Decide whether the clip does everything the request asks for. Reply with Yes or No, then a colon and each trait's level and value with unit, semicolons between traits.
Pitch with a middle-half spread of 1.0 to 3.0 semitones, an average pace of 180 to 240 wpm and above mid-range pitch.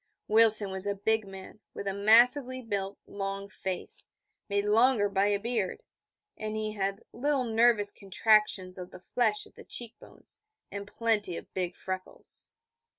No: narrow, 2.4 semitones; average, 155 wpm; high, 205 Hz